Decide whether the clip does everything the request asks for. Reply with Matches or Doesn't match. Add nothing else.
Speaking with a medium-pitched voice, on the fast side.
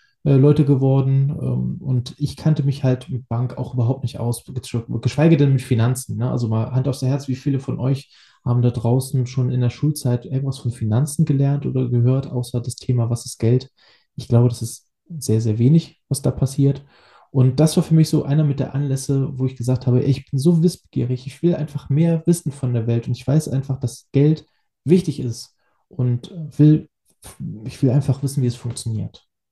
Doesn't match